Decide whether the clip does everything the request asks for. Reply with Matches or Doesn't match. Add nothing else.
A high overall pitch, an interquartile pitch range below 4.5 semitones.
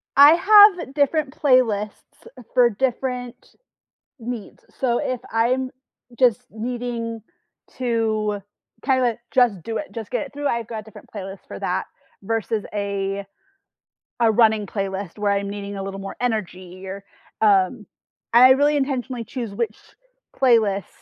Matches